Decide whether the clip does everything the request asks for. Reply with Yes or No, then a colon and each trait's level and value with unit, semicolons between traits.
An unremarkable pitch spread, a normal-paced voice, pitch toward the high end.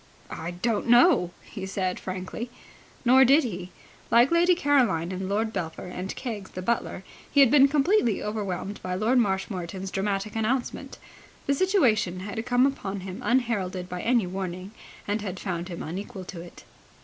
Yes: average, 4.9 semitones; average, 160 wpm; high, 205 Hz